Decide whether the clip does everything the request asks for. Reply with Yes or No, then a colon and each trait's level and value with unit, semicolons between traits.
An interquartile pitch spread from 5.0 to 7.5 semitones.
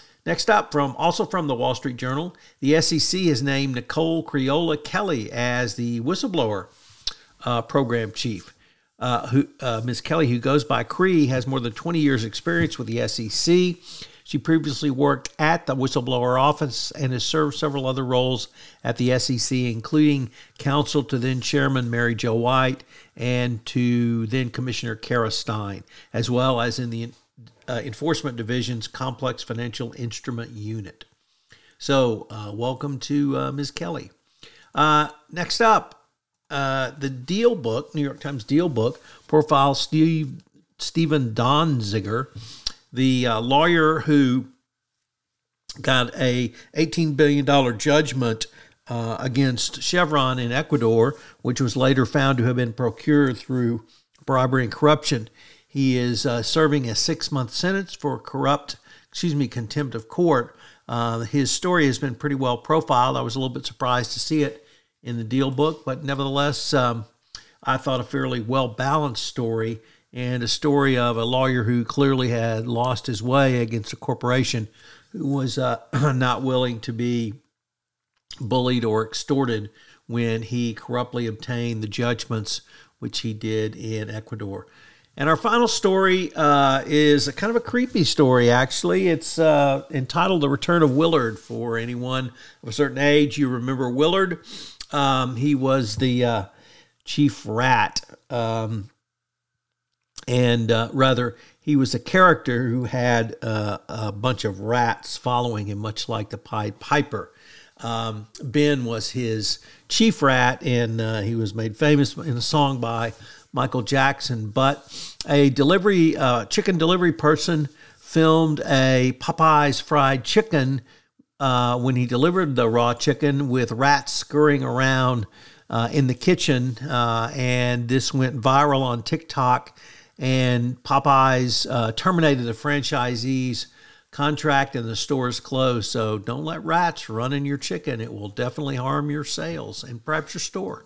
No: average, 3.7 semitones